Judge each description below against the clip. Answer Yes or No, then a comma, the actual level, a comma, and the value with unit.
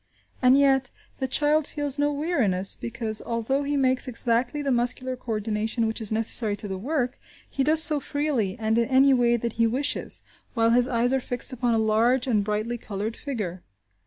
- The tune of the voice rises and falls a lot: No, average, 3.5 semitones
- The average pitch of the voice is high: Yes, high, 245 Hz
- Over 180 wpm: Yes, average, 190 wpm